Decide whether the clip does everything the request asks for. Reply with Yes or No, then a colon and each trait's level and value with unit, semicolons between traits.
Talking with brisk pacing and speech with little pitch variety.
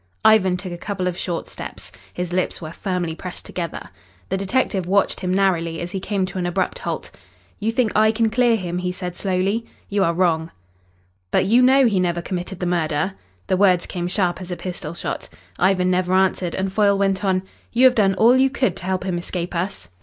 Yes: fast, 215 wpm; narrow, 2.2 semitones